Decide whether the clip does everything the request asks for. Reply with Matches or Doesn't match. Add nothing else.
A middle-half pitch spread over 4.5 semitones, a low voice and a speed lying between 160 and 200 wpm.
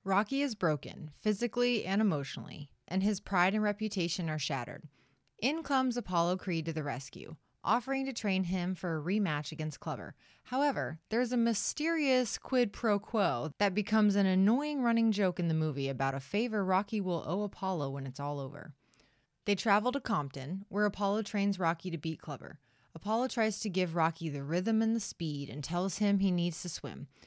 Doesn't match